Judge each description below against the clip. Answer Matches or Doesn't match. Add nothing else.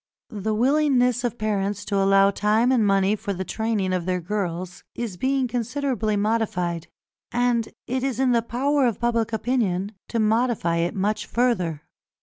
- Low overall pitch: Doesn't match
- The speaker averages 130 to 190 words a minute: Matches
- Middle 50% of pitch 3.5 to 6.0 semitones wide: Matches